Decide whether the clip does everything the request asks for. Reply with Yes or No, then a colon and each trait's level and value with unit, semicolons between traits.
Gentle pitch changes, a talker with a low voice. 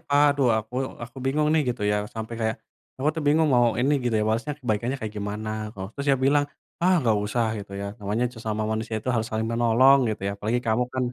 No: average, 3.6 semitones; low, 115 Hz